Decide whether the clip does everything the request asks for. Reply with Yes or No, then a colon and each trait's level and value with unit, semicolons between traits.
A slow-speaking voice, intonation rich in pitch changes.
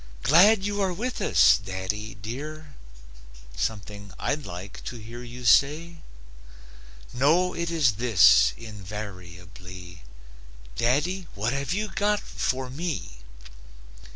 Yes: slow, 110 wpm; wide, 8.8 semitones